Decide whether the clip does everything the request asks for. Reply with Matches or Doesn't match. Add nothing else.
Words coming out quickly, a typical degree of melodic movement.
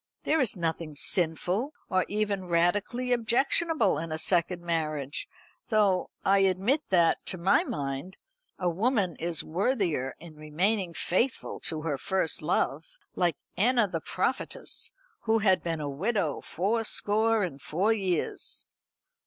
Doesn't match